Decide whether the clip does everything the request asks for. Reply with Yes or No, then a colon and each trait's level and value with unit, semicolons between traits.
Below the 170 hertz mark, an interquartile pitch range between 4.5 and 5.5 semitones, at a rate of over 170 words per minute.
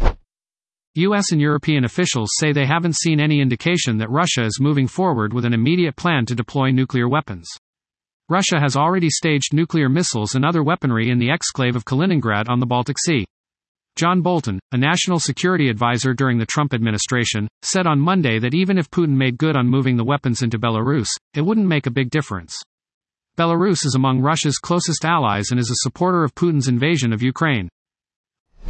Yes: medium, 140 Hz; average, 5.2 semitones; average, 180 wpm